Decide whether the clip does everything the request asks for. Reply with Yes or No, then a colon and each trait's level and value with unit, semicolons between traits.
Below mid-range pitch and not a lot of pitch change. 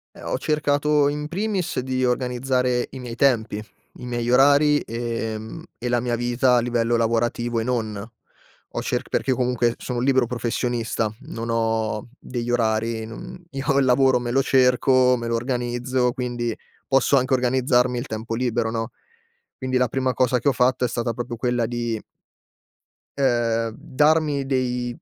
Yes: low, 125 Hz; narrow, 1.9 semitones